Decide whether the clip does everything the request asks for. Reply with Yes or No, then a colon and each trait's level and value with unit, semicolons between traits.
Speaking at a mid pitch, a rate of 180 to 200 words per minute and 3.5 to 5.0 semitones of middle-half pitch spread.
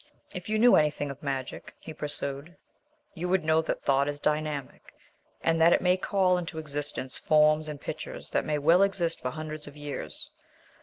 No: medium, 155 Hz; average, 185 wpm; average, 2.9 semitones